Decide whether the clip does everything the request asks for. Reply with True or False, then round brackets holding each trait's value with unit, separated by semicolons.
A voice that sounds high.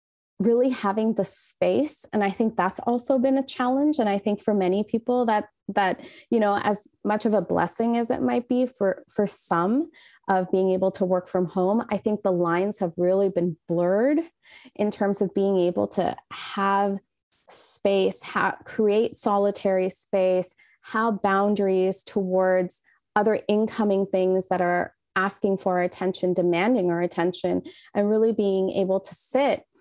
True (200 Hz)